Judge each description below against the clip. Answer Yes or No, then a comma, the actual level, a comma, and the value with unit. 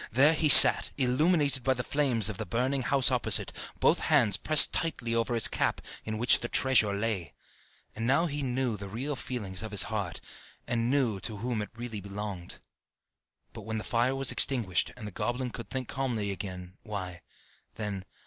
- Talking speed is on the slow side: No, average, 185 wpm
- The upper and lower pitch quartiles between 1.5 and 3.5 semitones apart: No, average, 4.1 semitones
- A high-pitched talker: No, low, 115 Hz